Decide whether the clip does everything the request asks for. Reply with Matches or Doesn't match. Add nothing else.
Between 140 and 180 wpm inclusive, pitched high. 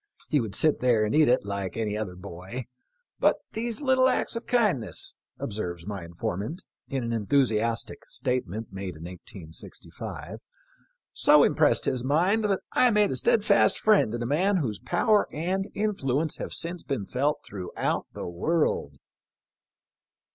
Doesn't match